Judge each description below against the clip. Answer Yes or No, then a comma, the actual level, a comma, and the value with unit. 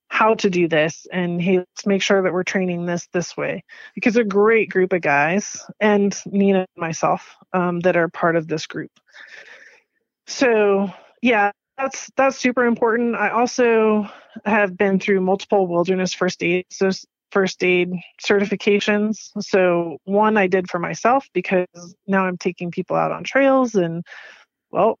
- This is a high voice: Yes, high, 195 Hz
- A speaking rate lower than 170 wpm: Yes, average, 160 wpm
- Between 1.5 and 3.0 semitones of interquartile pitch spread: Yes, average, 2.7 semitones